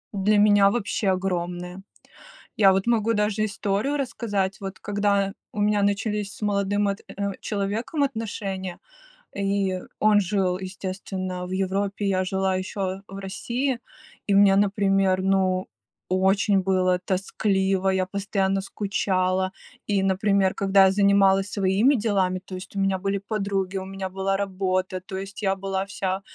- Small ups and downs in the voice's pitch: Yes, narrow, 1.2 semitones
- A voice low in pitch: No, high, 195 Hz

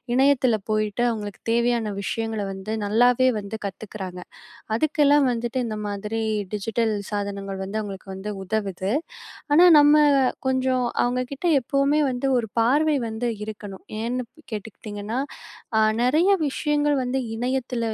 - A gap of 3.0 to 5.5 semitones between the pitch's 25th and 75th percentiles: Yes, average, 4.0 semitones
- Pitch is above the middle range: Yes, high, 230 Hz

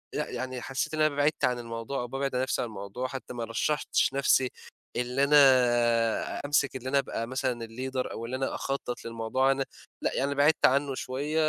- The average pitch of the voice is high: No, low, 130 Hz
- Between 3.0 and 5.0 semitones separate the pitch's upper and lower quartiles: No, narrow, 2.4 semitones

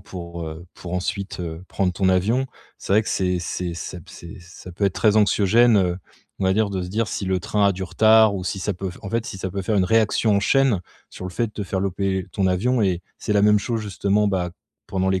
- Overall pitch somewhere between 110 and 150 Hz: No, very low, 95 Hz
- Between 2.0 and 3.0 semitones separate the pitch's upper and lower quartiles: Yes, narrow, 2.4 semitones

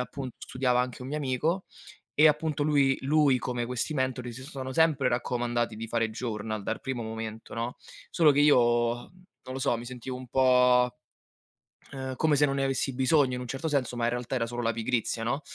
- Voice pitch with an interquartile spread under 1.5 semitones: No, narrow, 2.5 semitones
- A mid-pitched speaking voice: No, low, 130 Hz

